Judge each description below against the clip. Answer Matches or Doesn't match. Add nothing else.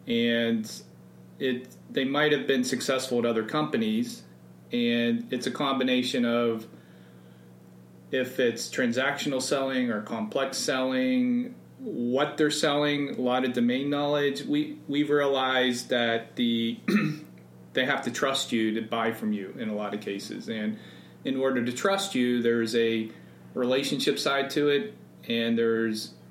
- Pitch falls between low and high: Doesn't match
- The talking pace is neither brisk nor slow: Matches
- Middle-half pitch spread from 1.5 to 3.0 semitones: Doesn't match